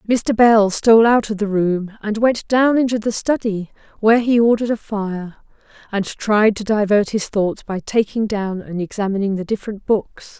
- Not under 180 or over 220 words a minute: Yes, average, 185 wpm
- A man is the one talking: No, female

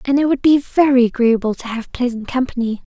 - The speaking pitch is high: Yes, very high, 250 Hz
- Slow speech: No, fast, 205 wpm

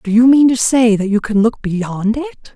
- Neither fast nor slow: No, fast, 260 wpm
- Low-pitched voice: No, high, 230 Hz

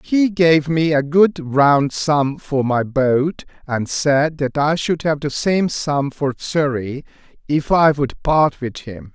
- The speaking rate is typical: Yes, average, 175 wpm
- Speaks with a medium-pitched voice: Yes, medium, 145 Hz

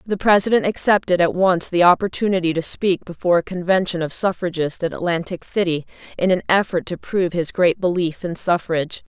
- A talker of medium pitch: Yes, medium, 180 Hz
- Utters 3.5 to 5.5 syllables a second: No, 5.7 syllables/s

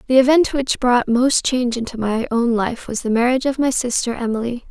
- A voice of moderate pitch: No, high, 245 Hz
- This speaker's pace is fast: Yes, fast, 215 wpm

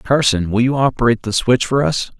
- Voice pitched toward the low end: Yes, low, 120 Hz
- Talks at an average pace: No, fast, 220 wpm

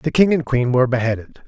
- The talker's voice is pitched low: Yes, low, 130 Hz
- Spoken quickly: Yes, fast, 245 wpm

